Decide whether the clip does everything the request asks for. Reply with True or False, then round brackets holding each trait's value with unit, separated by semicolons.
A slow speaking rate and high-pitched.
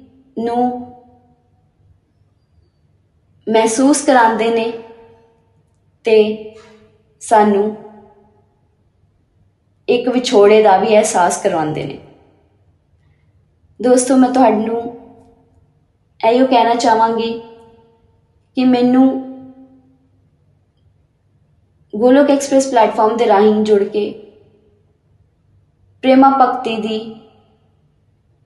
True (65 wpm; 220 Hz)